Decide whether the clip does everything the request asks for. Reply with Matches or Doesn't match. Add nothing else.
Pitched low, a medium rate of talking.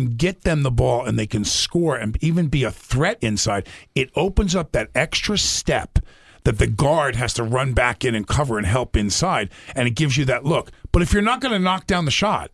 Doesn't match